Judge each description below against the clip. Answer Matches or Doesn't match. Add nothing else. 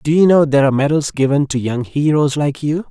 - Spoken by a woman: Doesn't match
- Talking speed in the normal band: Doesn't match